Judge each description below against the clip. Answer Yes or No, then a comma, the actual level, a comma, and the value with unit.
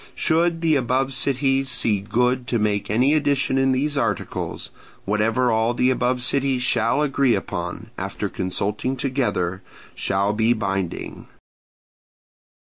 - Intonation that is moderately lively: Yes, average, 4.1 semitones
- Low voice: Yes, low, 125 Hz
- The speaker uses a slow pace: Yes, slow, 130 wpm